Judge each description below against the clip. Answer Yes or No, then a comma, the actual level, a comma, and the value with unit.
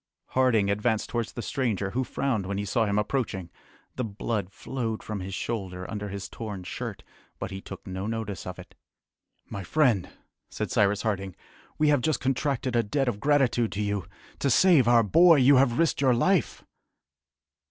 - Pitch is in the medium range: No, low, 115 Hz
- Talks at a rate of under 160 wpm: No, average, 180 wpm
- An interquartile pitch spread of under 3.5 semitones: No, average, 4.7 semitones